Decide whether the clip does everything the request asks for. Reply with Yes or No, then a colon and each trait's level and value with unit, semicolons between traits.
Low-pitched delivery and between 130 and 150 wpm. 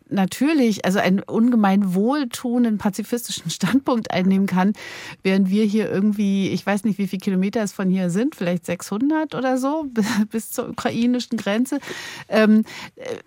No: high, 215 Hz; average, 145 wpm